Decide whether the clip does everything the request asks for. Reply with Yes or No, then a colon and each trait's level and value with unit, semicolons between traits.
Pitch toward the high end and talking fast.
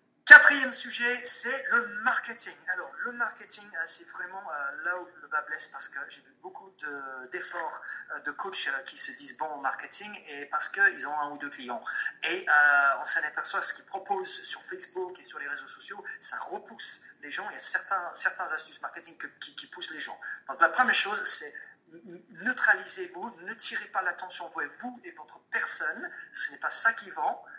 No: high, 210 Hz; average, 195 wpm